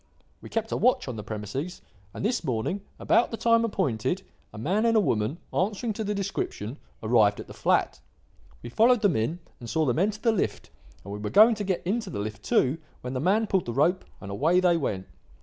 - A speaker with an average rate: No, fast, 220 wpm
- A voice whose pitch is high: No, medium, 175 Hz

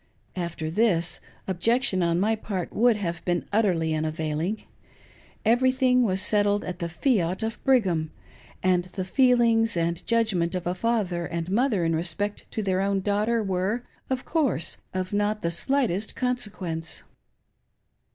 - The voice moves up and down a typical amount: Yes, average, 4.8 semitones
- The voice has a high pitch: Yes, high, 195 Hz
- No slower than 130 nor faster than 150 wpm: Yes, average, 140 wpm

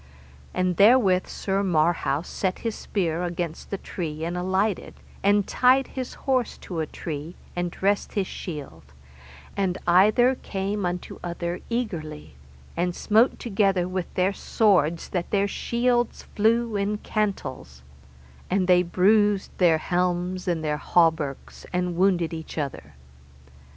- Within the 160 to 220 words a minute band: No, slow, 135 wpm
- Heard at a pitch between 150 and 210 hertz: Yes, medium, 185 Hz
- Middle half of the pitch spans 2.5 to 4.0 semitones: Yes, average, 3.2 semitones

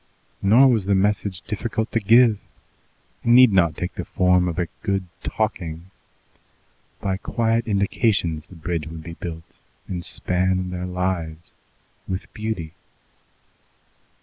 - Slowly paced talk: Yes, slow, 130 wpm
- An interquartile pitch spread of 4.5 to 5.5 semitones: No, average, 3.7 semitones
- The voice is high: No, very low, 95 Hz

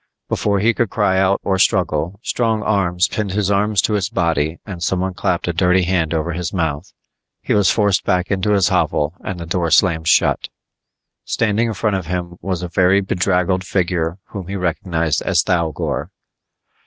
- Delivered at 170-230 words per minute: Yes, average, 180 wpm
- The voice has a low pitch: Yes, very low, 90 Hz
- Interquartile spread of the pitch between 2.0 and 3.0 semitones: Yes, narrow, 2.6 semitones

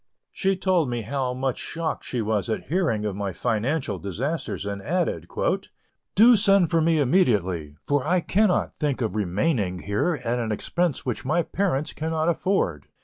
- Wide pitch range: Yes, wide, 8.2 semitones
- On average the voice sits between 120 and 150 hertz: Yes, low, 135 Hz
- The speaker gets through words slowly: No, average, 165 wpm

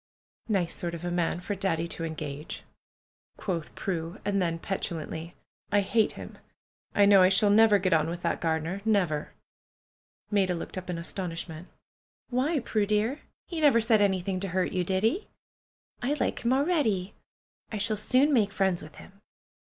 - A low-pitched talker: No, high, 190 Hz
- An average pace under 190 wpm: Yes, average, 175 wpm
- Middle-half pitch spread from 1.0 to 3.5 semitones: No, average, 4.1 semitones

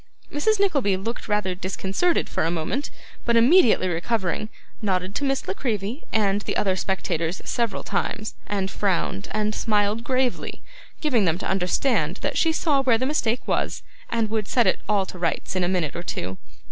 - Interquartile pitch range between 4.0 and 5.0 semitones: Yes, average, 4.6 semitones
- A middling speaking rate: Yes, average, 180 wpm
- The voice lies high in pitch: Yes, high, 210 Hz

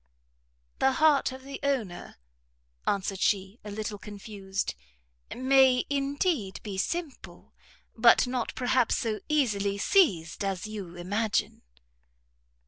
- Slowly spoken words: Yes, slow, 110 wpm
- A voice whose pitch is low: No, high, 220 Hz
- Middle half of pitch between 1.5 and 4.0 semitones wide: No, average, 5.1 semitones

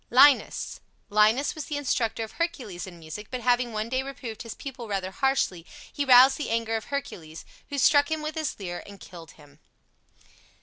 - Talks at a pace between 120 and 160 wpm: No, average, 185 wpm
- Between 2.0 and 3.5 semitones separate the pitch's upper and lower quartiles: No, wide, 5.5 semitones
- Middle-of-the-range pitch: No, high, 235 Hz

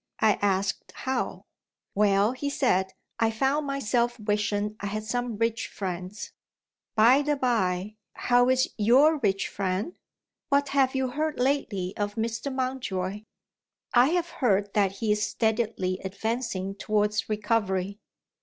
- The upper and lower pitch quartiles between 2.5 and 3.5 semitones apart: No, average, 4.2 semitones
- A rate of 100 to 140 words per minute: Yes, slow, 135 wpm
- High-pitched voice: Yes, high, 220 Hz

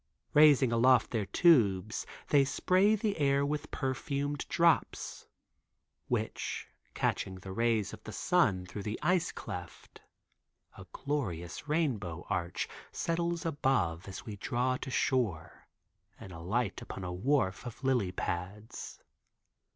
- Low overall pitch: Yes, low, 120 Hz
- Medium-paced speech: No, slow, 125 wpm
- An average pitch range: No, wide, 7.3 semitones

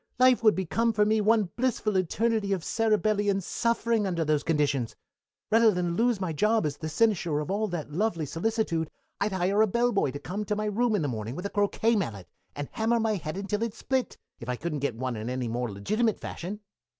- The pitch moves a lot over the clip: Yes, wide, 6.2 semitones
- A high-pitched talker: Yes, high, 200 Hz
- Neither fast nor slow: No, fast, 210 wpm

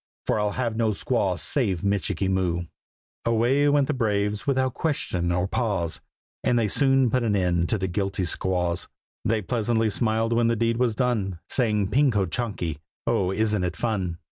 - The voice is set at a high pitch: No, low, 105 Hz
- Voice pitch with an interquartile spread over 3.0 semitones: Yes, average, 4.2 semitones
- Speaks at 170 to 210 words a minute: Yes, average, 175 wpm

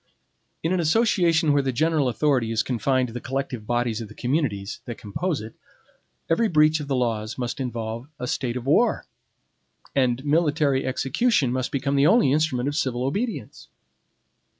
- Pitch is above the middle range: No, low, 135 Hz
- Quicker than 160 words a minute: Yes, average, 170 wpm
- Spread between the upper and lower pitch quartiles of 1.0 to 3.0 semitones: No, average, 4.1 semitones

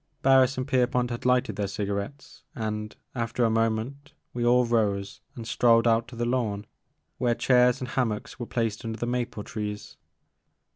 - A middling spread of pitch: No, narrow, 2.3 semitones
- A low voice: Yes, low, 120 Hz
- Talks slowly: No, average, 165 wpm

